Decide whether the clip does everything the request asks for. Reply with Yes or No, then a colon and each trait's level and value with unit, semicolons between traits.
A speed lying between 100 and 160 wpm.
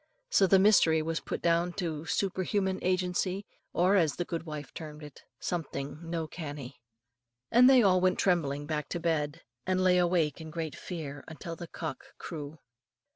No: average, 175 wpm